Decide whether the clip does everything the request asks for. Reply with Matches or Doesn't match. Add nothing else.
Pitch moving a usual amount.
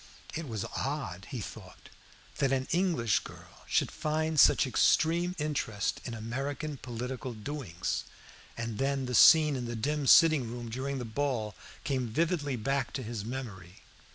Matches